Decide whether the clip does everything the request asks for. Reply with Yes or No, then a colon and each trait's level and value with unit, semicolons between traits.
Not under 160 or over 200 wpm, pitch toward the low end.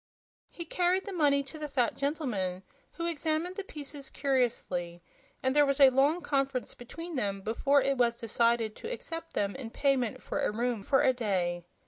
No: average, 180 wpm; very high, 270 Hz